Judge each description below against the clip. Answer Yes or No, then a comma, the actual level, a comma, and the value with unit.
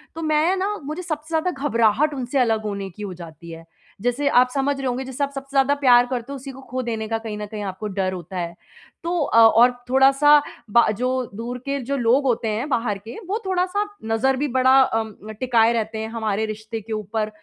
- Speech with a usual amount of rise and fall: Yes, average, 4.2 semitones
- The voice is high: Yes, high, 245 Hz